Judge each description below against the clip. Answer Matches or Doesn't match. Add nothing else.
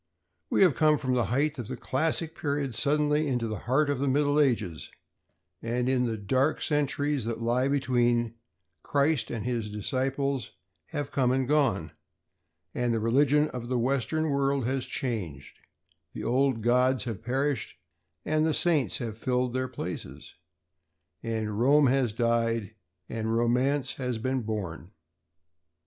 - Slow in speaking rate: Doesn't match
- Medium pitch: Doesn't match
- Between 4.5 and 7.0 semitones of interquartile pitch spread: Doesn't match